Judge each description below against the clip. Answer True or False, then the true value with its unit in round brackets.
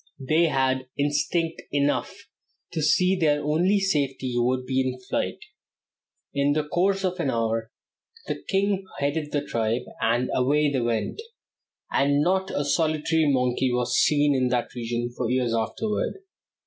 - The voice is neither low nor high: True (145 Hz)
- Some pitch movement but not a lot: True (4.2 semitones)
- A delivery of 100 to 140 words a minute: False (150 wpm)